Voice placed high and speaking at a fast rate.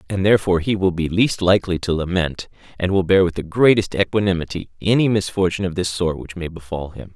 No: very low, 90 Hz; fast, 210 wpm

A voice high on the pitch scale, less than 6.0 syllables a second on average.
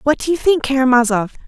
No: very high, 265 Hz; 6.4 syllables/s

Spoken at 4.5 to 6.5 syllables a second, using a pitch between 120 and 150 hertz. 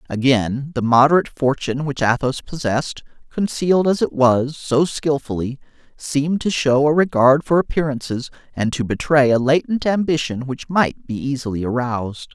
Yes: 5.1 syllables/s; low, 135 Hz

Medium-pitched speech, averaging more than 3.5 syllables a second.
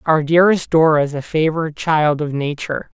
Yes: medium, 155 Hz; 6.0 syllables/s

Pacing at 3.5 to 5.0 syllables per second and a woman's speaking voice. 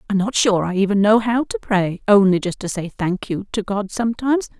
No: 5.6 syllables/s; female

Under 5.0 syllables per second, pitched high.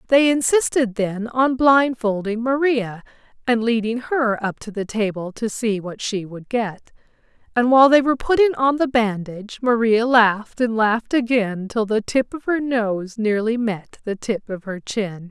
Yes: 4.5 syllables/s; high, 230 Hz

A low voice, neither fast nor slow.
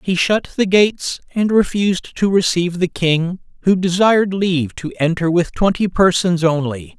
No: medium, 180 Hz; average, 165 wpm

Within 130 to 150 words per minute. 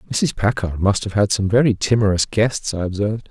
No: average, 200 wpm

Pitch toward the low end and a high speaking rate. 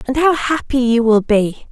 No: very high, 250 Hz; fast, 210 wpm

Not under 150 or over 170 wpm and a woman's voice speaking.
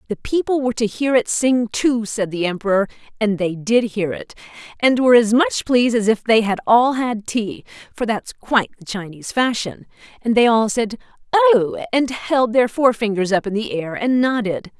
No: average, 200 wpm; female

